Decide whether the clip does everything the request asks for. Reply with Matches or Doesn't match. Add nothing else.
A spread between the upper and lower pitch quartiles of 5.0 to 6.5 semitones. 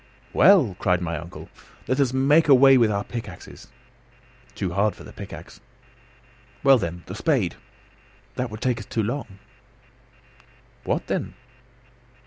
Matches